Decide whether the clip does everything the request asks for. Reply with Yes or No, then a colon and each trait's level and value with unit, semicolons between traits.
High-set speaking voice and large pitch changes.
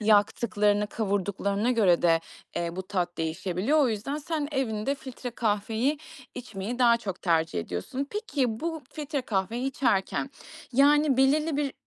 Yes: high, 225 Hz; wide, 5.8 semitones